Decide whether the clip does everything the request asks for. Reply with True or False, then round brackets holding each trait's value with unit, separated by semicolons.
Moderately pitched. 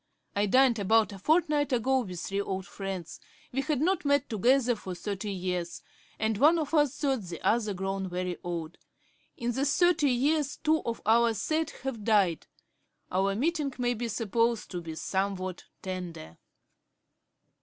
False (225 Hz)